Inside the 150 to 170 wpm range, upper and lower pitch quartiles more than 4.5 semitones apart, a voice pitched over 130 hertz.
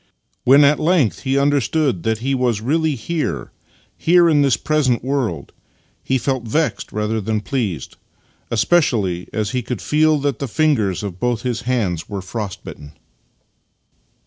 No: average, 155 wpm; average, 5.2 semitones; low, 125 Hz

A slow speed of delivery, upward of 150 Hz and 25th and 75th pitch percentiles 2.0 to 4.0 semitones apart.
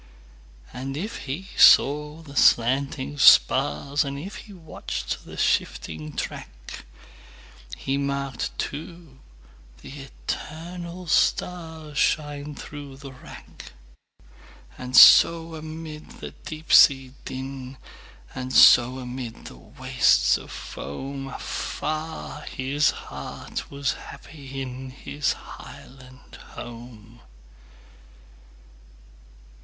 No: slow, 80 wpm; medium, 140 Hz; average, 3.2 semitones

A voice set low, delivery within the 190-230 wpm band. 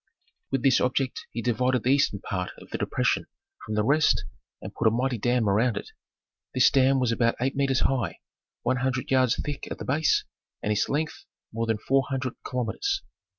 Yes: low, 125 Hz; average, 195 wpm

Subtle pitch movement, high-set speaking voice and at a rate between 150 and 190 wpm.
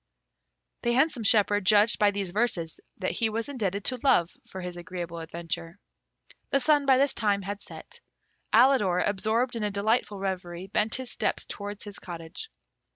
No: average, 4.3 semitones; high, 205 Hz; average, 165 wpm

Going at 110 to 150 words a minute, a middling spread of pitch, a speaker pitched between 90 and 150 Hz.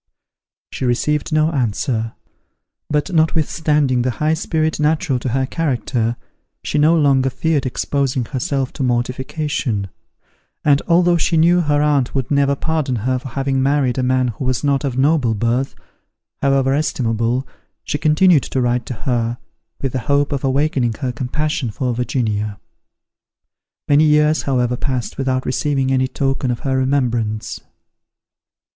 Yes: average, 145 wpm; average, 3.2 semitones; low, 135 Hz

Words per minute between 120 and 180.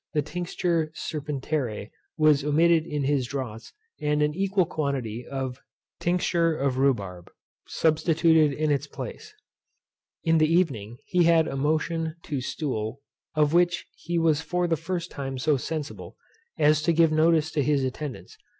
Yes: average, 150 wpm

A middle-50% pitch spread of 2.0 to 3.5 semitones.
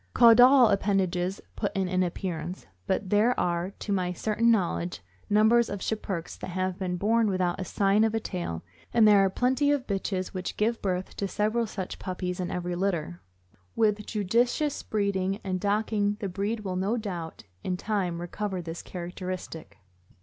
Yes: average, 2.9 semitones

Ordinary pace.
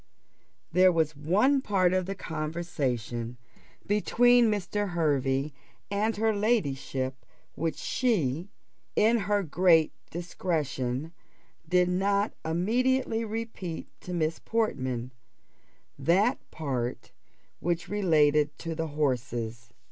No: slow, 100 wpm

